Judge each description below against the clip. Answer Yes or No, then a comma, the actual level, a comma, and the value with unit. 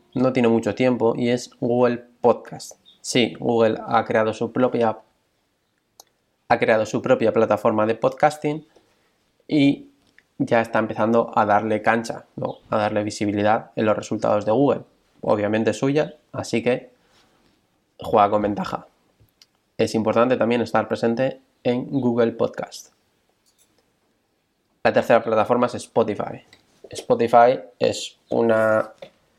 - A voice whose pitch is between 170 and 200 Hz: No, low, 115 Hz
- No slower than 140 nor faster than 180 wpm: No, slow, 125 wpm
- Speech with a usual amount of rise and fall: No, narrow, 2.1 semitones